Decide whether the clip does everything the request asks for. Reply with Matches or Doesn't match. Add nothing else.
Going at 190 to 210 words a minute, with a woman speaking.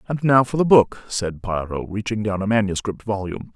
Doesn't match